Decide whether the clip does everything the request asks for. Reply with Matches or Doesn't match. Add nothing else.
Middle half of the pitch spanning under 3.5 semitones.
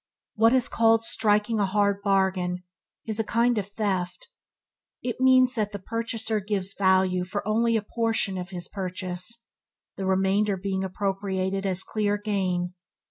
Matches